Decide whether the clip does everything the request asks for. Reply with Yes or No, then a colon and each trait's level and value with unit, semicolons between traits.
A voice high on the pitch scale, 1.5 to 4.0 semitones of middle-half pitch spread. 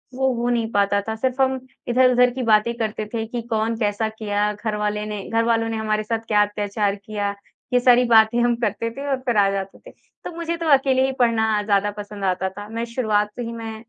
Yes: high, 220 Hz; narrow, 2.5 semitones